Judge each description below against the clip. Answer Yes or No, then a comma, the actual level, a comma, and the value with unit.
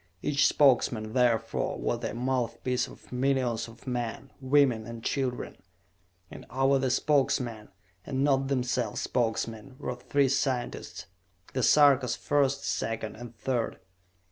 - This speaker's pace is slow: Yes, slow, 125 wpm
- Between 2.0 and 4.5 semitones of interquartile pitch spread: Yes, average, 2.8 semitones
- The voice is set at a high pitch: No, low, 125 Hz